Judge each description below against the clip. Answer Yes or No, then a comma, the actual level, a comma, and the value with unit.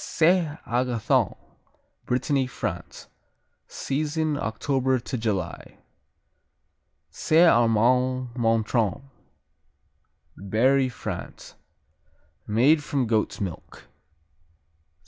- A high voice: No, low, 125 Hz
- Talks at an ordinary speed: No, slow, 70 wpm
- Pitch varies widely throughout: No, average, 3.9 semitones